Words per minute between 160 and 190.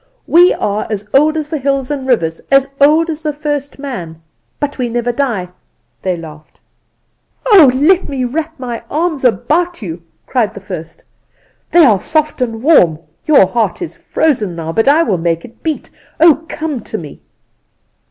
Yes: average, 170 wpm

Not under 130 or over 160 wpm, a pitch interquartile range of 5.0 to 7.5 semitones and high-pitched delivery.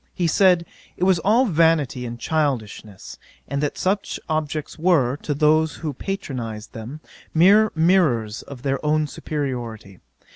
No: average, 140 wpm; average, 5.3 semitones; medium, 150 Hz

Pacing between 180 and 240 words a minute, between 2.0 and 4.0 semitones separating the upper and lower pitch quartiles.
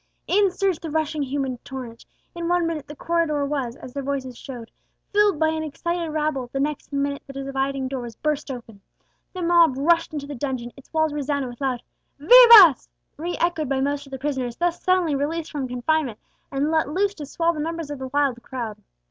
Yes: fast, 205 wpm; average, 3.7 semitones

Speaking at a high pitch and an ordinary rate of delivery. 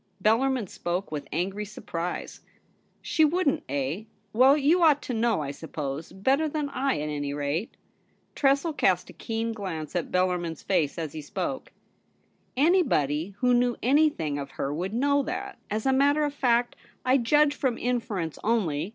Yes: high, 220 Hz; average, 170 wpm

